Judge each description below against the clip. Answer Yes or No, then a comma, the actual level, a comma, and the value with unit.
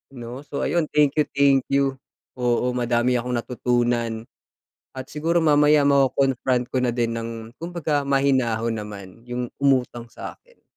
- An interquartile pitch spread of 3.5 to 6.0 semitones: No, average, 2.9 semitones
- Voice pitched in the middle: No, low, 125 Hz